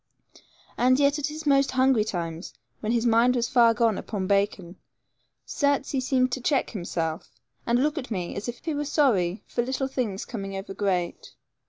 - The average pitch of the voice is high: Yes, high, 235 Hz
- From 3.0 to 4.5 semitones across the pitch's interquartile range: No, wide, 5.4 semitones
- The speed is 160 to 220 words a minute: Yes, average, 185 wpm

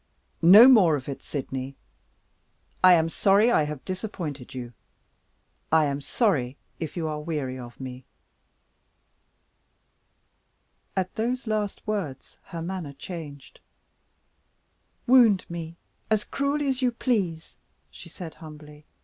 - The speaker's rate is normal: No, slow, 120 wpm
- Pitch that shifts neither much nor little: No, wide, 6.4 semitones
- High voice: No, medium, 165 Hz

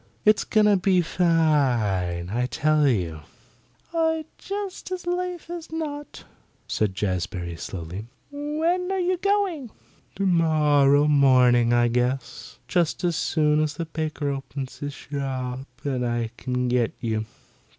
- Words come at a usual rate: No, slow, 130 wpm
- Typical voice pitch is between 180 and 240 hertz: No, medium, 145 Hz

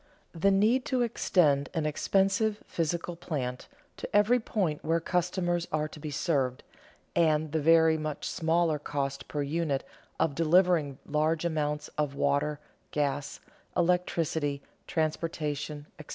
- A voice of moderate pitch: Yes, medium, 160 Hz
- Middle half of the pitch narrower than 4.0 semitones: Yes, average, 3.0 semitones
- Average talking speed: No, slow, 130 wpm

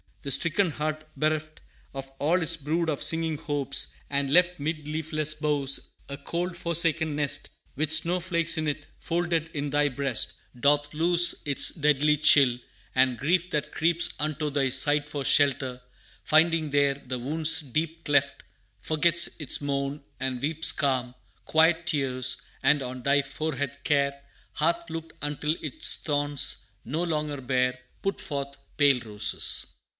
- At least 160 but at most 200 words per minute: No, average, 150 wpm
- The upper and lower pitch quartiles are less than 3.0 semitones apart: Yes, narrow, 2.5 semitones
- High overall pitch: No, medium, 150 Hz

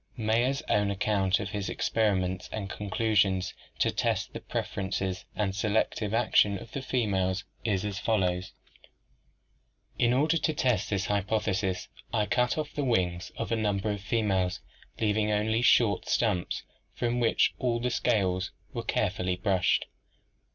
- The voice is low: Yes, low, 105 Hz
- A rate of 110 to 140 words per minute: No, average, 150 wpm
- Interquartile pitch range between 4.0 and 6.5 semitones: No, average, 3.2 semitones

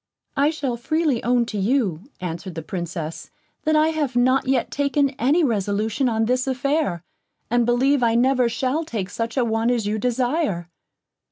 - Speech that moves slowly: No, average, 170 wpm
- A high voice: Yes, high, 245 Hz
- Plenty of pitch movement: No, average, 4.2 semitones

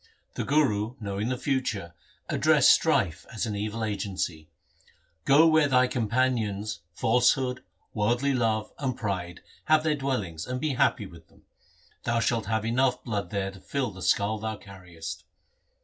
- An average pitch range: Yes, average, 4.5 semitones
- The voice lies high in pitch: No, low, 110 Hz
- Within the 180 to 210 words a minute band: No, average, 160 wpm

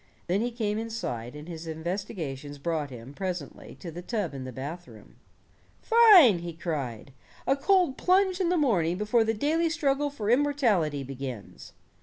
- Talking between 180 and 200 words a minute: No, average, 160 wpm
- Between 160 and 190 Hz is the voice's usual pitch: Yes, medium, 185 Hz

